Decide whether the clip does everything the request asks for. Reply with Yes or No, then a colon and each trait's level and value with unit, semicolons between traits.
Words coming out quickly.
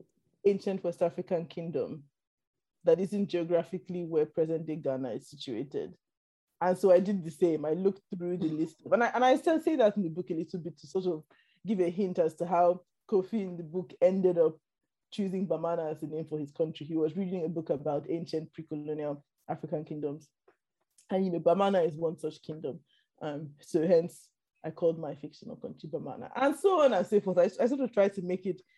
Yes: fast, 210 wpm